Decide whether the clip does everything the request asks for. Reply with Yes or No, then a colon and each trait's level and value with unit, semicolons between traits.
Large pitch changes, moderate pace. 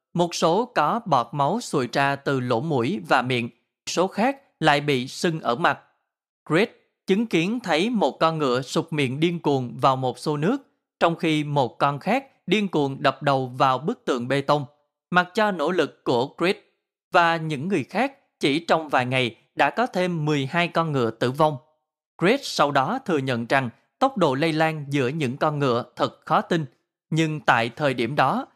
No: average, 4.3 semitones; average, 195 wpm